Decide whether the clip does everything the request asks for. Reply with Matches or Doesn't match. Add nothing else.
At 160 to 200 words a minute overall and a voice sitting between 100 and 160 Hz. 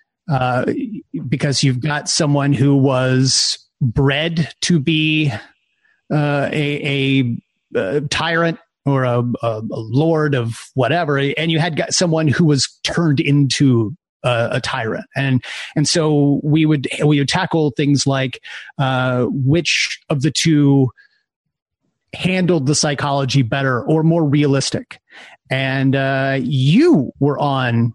Doesn't match